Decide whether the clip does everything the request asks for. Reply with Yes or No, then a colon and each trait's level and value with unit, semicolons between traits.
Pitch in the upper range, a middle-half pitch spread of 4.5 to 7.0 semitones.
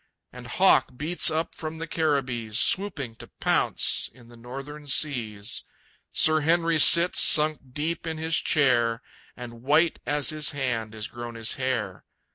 No: medium, 140 Hz; average, 4.8 semitones